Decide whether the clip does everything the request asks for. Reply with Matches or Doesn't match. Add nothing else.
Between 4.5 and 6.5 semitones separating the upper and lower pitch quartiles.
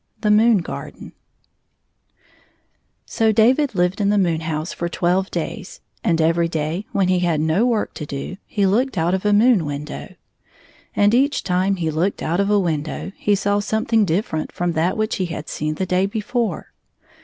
Doesn't match